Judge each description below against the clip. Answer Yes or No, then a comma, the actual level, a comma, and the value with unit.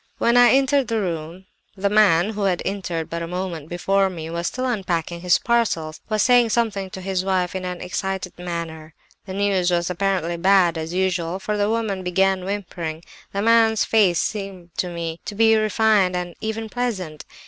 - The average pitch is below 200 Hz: Yes, high, 190 Hz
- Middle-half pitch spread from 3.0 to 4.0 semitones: Yes, average, 3.5 semitones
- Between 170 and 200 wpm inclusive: Yes, average, 190 wpm